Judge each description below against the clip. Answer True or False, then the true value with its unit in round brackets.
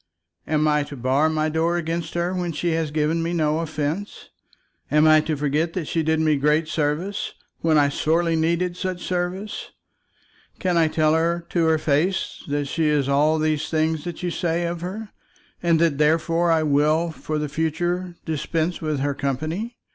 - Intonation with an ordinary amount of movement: False (2.1 semitones)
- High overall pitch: False (160 Hz)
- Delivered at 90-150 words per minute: False (185 wpm)